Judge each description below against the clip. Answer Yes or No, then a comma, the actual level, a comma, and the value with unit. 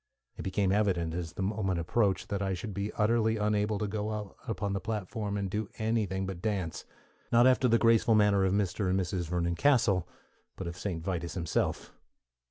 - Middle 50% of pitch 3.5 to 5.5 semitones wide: No, narrow, 2.6 semitones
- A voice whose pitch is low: Yes, low, 100 Hz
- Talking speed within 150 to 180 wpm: No, average, 190 wpm